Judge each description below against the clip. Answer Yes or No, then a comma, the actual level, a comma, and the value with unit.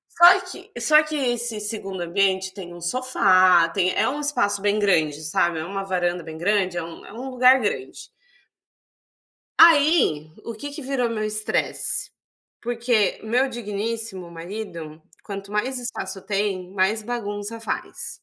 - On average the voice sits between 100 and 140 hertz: No, high, 205 Hz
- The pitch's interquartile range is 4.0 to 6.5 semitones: Yes, average, 4.7 semitones